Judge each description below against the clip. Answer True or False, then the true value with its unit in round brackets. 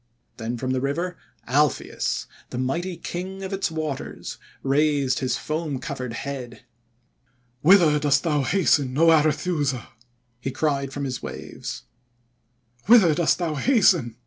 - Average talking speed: False (130 wpm)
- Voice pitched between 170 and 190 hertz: False (150 Hz)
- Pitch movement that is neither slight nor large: True (4.2 semitones)